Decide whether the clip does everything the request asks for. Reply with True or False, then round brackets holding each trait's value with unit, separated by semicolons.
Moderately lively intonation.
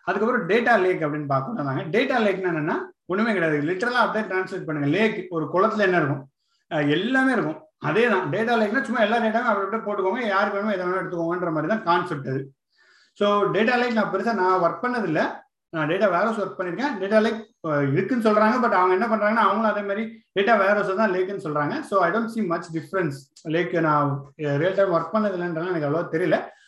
True (5.0 semitones)